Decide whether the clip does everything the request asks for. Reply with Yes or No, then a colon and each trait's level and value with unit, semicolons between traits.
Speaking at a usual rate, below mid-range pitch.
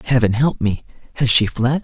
Yes: average, 195 wpm; low, 120 Hz